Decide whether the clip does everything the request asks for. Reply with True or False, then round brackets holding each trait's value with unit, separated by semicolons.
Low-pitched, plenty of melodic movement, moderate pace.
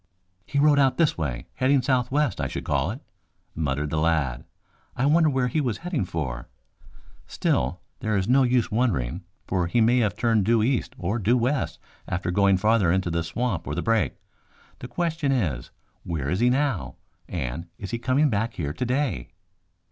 True (110 Hz; 7.4 semitones; 180 wpm)